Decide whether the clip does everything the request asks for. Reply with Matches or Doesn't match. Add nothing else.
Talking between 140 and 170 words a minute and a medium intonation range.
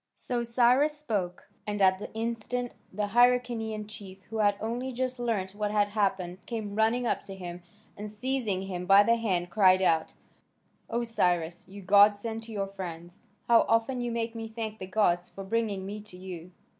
Doesn't match